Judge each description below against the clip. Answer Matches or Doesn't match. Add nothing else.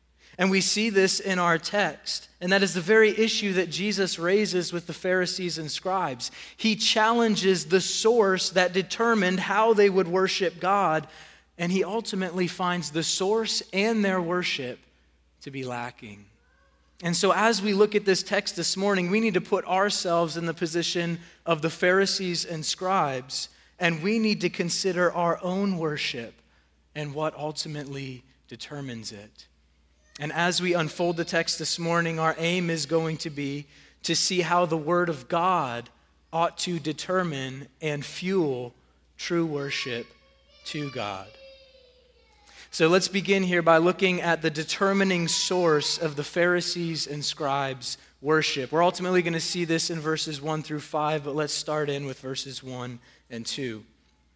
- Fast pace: Doesn't match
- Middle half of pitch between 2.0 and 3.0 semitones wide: Doesn't match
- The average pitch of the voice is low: Doesn't match